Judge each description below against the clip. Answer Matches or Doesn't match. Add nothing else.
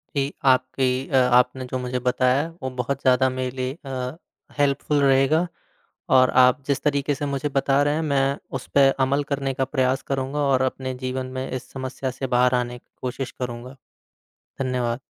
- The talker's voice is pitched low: Matches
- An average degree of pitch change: Doesn't match